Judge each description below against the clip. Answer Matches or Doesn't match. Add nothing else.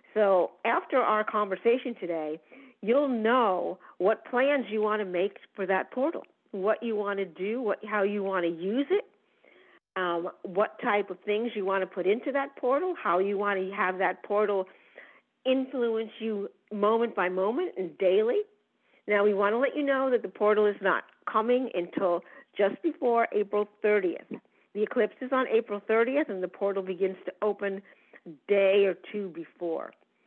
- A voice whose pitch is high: Matches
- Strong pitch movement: Doesn't match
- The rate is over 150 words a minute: Matches